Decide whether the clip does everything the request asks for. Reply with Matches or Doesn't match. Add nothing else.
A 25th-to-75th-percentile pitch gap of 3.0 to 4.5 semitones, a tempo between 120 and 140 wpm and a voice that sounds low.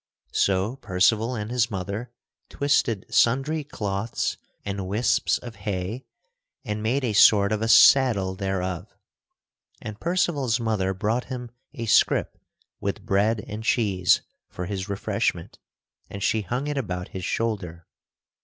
Matches